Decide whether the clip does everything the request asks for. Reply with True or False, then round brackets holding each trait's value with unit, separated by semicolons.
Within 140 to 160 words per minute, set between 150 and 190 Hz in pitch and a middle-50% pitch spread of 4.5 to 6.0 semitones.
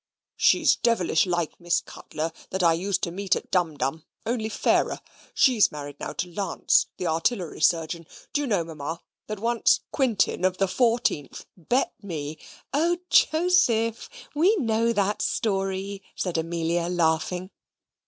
True (145 wpm; 185 Hz; 5.5 semitones)